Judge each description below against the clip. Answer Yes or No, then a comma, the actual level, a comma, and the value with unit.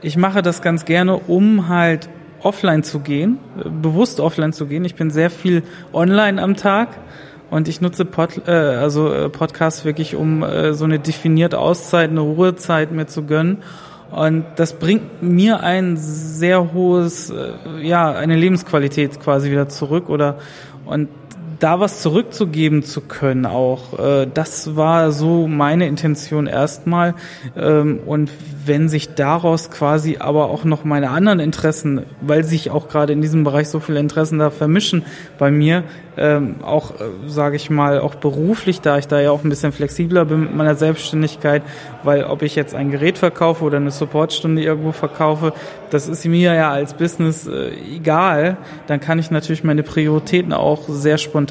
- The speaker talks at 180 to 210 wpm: No, average, 160 wpm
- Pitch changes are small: Yes, narrow, 2.2 semitones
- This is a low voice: No, medium, 155 Hz